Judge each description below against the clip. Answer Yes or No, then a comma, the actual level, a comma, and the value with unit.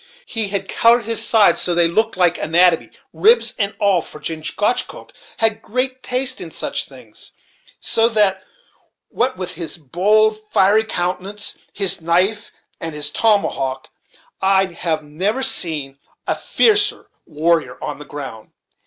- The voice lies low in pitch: No, high, 190 Hz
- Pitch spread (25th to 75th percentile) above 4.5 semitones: Yes, average, 5.2 semitones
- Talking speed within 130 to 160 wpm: Yes, average, 145 wpm